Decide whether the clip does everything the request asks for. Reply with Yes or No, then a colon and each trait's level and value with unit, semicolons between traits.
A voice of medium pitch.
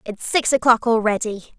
No: high, 230 Hz